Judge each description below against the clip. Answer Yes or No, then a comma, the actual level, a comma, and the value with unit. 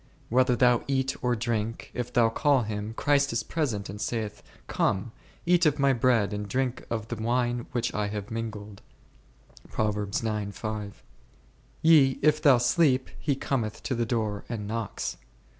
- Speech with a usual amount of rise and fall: Yes, average, 3.5 semitones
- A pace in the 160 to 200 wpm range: No, average, 150 wpm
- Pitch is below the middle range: Yes, low, 115 Hz